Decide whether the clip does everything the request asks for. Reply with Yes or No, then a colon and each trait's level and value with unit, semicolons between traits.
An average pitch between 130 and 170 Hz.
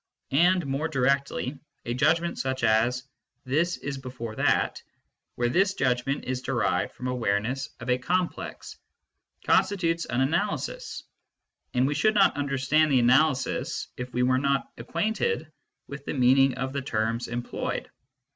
Yes: low, 135 Hz